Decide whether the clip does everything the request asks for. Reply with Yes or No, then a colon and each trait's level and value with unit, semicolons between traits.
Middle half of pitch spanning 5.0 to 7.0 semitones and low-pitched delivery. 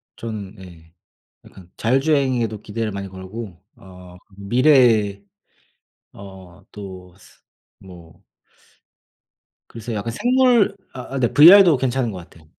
Yes: wide, 5.4 semitones; low, 105 Hz